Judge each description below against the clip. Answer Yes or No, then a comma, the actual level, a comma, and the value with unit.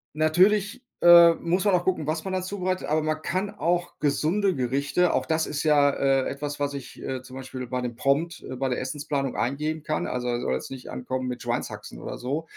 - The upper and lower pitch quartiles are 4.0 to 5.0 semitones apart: Yes, average, 4.6 semitones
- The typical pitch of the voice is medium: Yes, medium, 150 Hz